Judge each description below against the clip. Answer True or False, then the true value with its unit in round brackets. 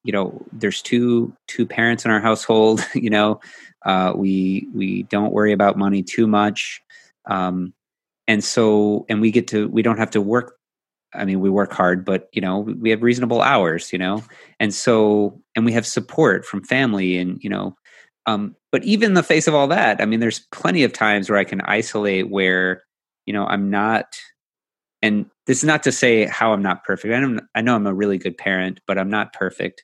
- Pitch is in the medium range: False (105 Hz)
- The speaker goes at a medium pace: False (210 wpm)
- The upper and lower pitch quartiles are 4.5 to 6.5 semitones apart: False (2.8 semitones)